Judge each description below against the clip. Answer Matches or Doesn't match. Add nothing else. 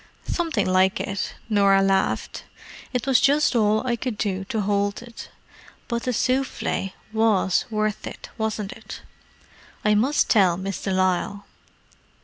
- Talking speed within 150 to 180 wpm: Doesn't match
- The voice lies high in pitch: Matches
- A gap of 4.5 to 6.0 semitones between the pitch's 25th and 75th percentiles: Doesn't match